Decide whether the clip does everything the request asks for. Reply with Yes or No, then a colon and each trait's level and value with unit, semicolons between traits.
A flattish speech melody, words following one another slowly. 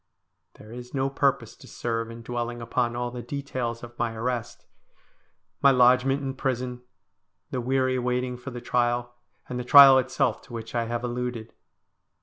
No: narrow, 1.6 semitones; average, 165 wpm